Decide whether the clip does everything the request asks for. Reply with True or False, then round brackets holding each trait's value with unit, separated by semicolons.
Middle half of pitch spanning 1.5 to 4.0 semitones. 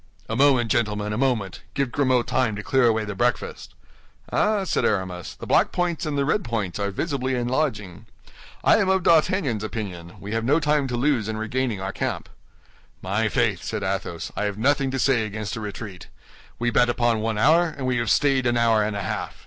False (4.4 semitones)